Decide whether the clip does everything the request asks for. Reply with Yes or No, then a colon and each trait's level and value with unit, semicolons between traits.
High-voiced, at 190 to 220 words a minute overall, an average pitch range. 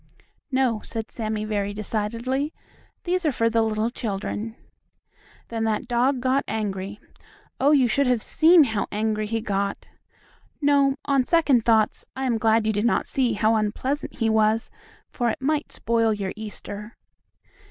No: high, 225 Hz; average, 155 wpm; average, 3.5 semitones